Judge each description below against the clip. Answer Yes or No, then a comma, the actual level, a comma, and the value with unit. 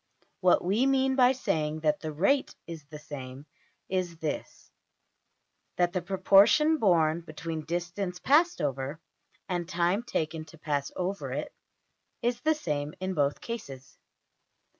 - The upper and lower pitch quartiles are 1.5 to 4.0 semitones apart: No, average, 4.6 semitones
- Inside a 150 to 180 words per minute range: No, average, 140 wpm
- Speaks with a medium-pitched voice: Yes, medium, 175 Hz